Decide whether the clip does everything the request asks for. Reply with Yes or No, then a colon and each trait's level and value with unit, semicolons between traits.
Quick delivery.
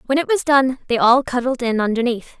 Yes: fast, 225 wpm